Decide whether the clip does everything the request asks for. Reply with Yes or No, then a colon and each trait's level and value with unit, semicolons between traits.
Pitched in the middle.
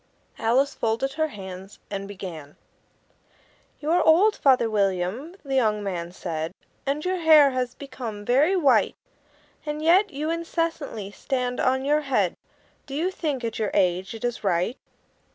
No: very high, 255 Hz